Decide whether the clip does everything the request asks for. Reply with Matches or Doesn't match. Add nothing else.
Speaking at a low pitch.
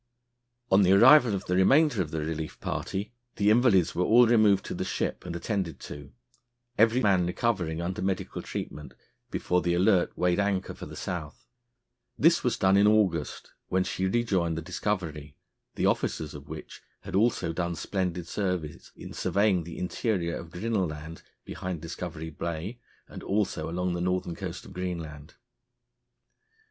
Matches